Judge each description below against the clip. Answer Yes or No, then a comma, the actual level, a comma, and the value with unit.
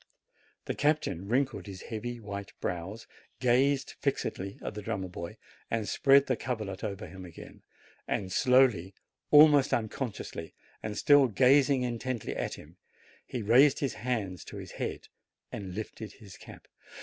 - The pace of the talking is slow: No, average, 145 wpm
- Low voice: Yes, low, 110 Hz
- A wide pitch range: No, average, 4.9 semitones